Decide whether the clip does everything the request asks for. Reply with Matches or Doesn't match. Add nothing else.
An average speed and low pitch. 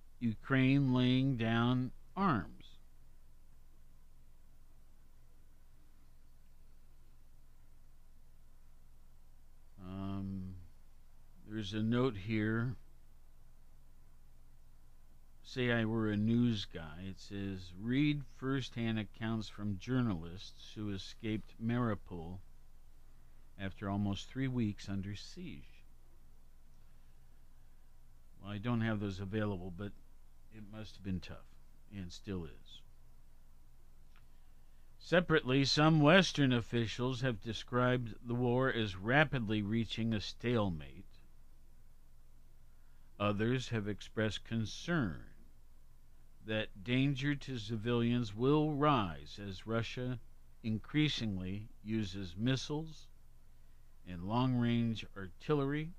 Doesn't match